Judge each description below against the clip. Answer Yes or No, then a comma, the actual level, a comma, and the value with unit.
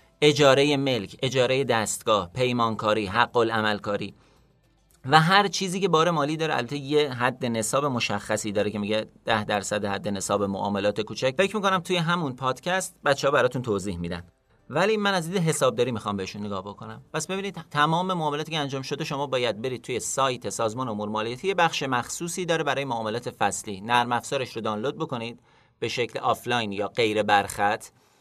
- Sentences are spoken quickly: Yes, fast, 165 wpm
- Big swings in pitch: Yes, wide, 5.8 semitones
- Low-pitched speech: Yes, low, 125 Hz